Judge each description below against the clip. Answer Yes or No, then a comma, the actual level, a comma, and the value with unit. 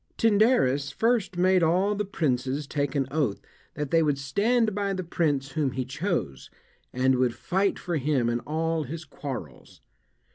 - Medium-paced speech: Yes, average, 160 wpm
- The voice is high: No, medium, 155 Hz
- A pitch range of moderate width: No, wide, 5.8 semitones